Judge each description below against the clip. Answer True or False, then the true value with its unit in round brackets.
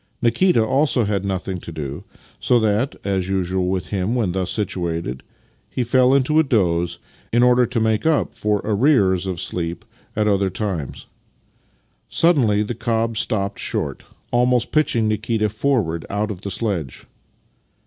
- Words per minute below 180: True (150 wpm)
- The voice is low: True (105 Hz)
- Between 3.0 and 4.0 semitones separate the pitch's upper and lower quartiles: False (4.5 semitones)